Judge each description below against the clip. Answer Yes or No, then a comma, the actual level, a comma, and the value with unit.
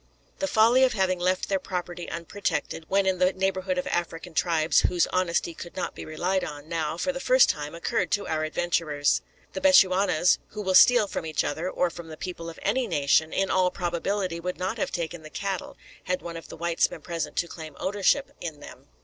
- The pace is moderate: No, fast, 210 wpm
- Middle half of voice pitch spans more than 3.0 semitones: No, narrow, 2.6 semitones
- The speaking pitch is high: No, medium, 180 Hz